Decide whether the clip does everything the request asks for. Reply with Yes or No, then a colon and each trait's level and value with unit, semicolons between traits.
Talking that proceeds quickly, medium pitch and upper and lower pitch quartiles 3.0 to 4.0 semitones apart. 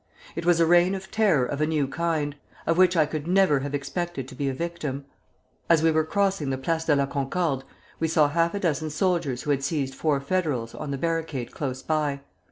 Yes: fast, 220 wpm; medium, 155 Hz; average, 3.4 semitones